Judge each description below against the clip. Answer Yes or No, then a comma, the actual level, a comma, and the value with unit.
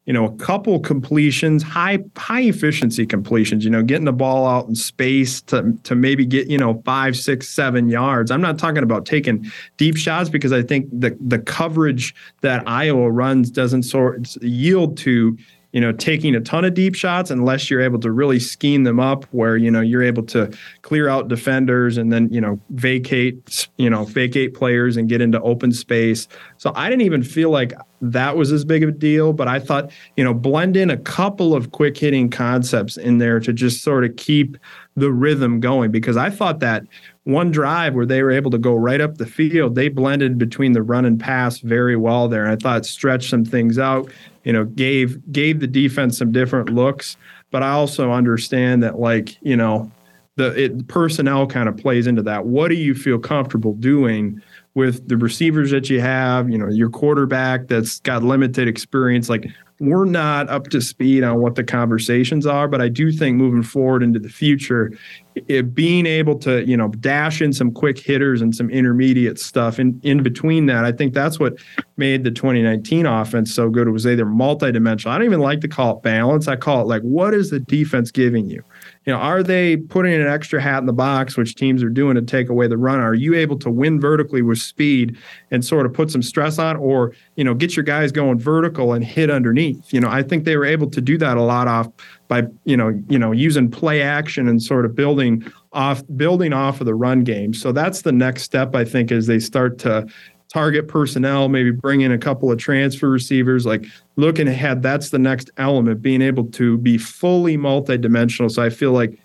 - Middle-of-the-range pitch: No, low, 130 Hz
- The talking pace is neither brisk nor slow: No, fast, 215 wpm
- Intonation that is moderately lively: Yes, average, 3.3 semitones